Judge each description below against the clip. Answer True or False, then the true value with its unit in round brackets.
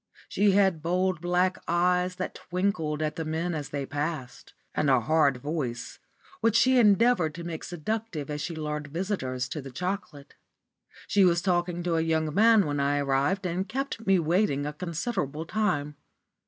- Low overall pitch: False (170 Hz)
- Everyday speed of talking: True (170 wpm)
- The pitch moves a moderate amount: True (4.1 semitones)